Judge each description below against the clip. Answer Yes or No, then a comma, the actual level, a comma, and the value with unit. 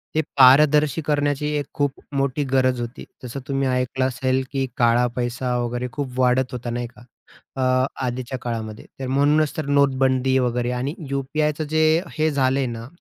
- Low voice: Yes, low, 130 Hz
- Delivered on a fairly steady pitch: Yes, narrow, 2.2 semitones